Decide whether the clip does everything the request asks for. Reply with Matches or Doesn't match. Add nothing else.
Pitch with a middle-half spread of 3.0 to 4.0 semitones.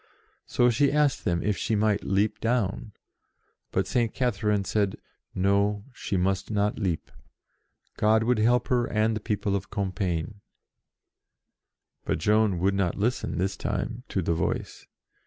Doesn't match